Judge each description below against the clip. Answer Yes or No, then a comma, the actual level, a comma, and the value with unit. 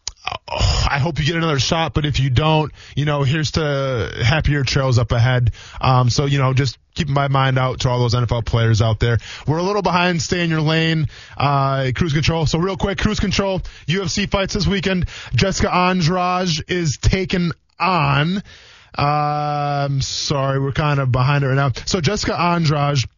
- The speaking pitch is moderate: Yes, medium, 145 Hz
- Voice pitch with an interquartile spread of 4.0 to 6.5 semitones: Yes, average, 4.6 semitones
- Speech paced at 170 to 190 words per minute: Yes, average, 185 wpm